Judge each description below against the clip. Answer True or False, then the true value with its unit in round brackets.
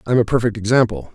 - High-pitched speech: False (115 Hz)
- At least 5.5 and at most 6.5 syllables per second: False (6.9 syllables/s)